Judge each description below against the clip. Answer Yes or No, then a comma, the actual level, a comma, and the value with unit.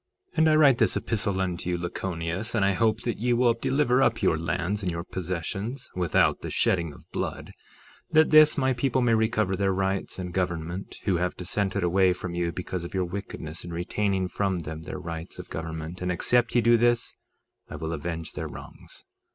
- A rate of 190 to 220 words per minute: Yes, average, 200 wpm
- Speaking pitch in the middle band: No, very low, 95 Hz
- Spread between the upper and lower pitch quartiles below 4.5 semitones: No, average, 5.0 semitones